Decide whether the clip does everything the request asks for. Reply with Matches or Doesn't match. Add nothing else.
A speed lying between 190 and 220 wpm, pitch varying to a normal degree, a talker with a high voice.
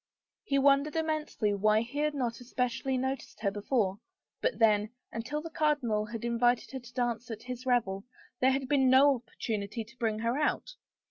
Matches